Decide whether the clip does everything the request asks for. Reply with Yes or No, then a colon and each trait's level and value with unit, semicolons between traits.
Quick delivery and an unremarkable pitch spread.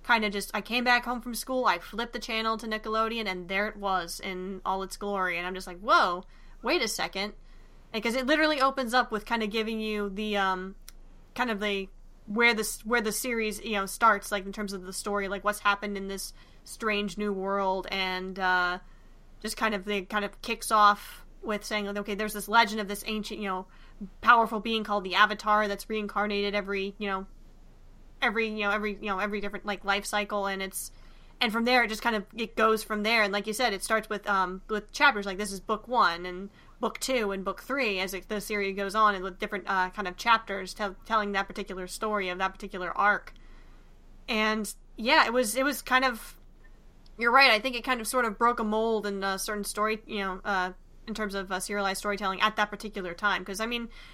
No: fast, 230 wpm; narrow, 2.2 semitones